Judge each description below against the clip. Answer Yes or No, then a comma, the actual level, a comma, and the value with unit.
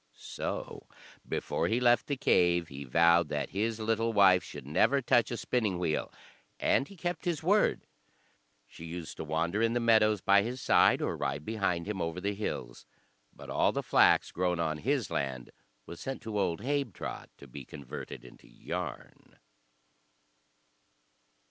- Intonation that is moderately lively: No, wide, 5.8 semitones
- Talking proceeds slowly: No, average, 160 wpm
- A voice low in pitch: Yes, low, 100 Hz